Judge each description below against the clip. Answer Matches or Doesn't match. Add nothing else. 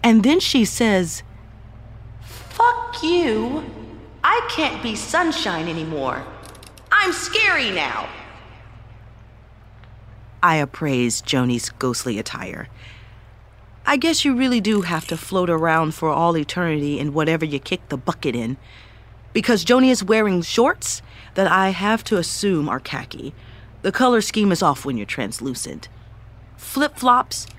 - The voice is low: Doesn't match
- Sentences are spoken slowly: Matches